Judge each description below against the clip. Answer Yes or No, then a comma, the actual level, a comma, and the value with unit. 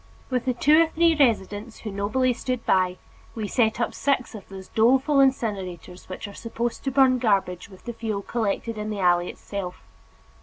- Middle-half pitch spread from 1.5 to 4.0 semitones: No, average, 4.4 semitones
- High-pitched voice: Yes, high, 225 Hz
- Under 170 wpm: No, average, 185 wpm